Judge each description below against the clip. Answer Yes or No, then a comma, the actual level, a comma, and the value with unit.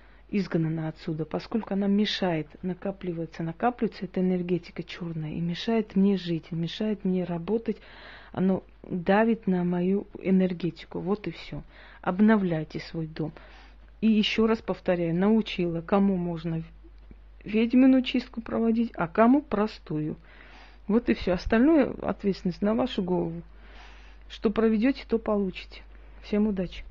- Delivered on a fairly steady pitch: No, average, 4.2 semitones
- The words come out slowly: No, average, 125 wpm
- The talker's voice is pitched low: No, medium, 185 Hz